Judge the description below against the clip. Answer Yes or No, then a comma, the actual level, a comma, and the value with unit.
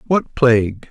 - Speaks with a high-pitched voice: No, low, 125 Hz